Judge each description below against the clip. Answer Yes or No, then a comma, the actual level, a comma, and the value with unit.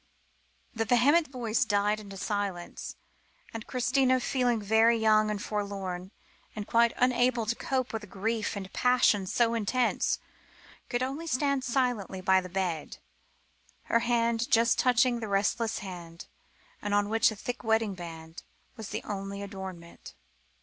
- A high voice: Yes, high, 220 Hz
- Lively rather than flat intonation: No, average, 3.5 semitones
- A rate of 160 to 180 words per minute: No, average, 145 wpm